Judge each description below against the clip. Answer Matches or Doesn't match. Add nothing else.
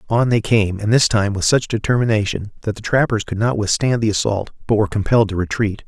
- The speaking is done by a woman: Doesn't match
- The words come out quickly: Matches